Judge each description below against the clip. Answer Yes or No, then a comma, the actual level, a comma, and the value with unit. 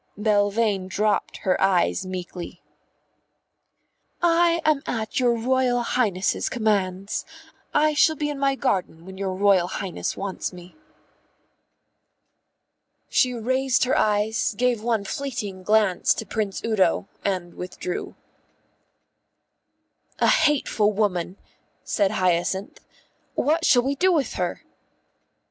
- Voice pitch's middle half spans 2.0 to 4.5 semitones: No, average, 5.1 semitones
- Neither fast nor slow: No, slow, 115 wpm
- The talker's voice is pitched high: Yes, high, 210 Hz